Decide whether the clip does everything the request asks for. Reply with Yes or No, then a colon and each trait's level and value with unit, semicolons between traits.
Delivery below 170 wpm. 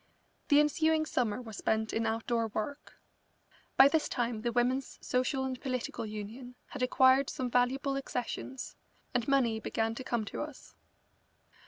Yes: average, 150 wpm